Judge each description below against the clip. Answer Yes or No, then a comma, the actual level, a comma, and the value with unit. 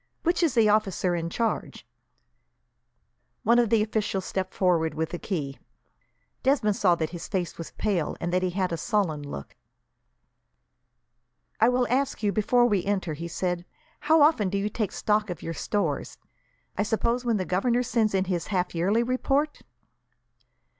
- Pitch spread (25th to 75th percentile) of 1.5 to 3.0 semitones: No, average, 4.8 semitones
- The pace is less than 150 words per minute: No, average, 165 wpm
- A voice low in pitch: No, high, 205 Hz